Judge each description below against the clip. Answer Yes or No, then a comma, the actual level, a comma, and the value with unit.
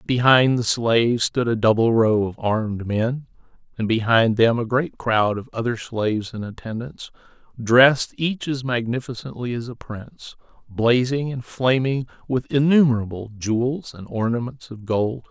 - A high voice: No, low, 120 Hz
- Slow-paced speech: No, average, 150 wpm